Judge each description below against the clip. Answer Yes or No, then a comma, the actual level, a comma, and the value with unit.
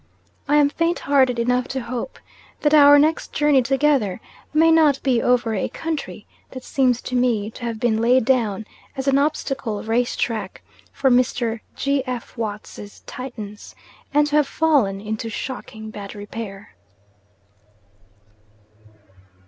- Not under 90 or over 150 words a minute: Yes, average, 140 wpm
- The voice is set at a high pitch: Yes, very high, 250 Hz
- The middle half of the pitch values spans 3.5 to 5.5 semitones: Yes, average, 4.3 semitones